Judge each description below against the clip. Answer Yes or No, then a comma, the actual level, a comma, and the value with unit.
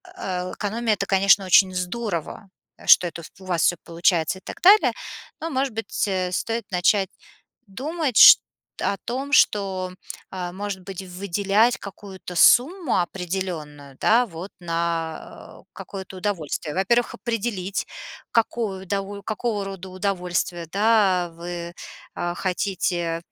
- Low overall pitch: No, high, 190 Hz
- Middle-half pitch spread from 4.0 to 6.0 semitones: No, average, 3.2 semitones